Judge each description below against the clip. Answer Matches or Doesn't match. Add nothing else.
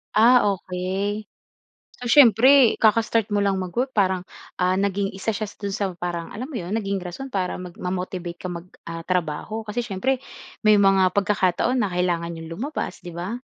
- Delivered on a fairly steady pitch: Doesn't match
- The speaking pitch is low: Doesn't match